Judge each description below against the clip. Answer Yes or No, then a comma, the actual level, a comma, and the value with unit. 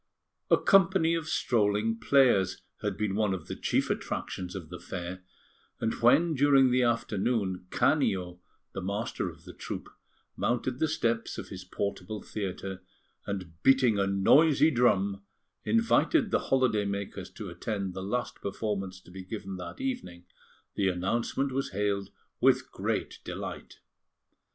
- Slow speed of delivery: No, average, 145 wpm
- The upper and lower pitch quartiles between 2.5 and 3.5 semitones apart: No, average, 5.1 semitones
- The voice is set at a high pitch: No, low, 105 Hz